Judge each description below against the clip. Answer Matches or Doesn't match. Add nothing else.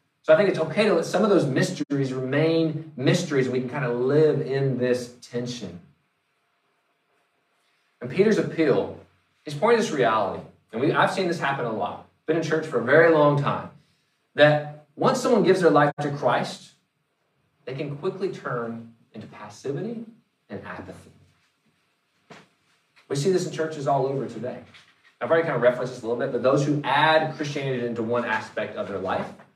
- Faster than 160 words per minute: Matches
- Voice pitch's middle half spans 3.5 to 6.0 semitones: Matches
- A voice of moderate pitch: Matches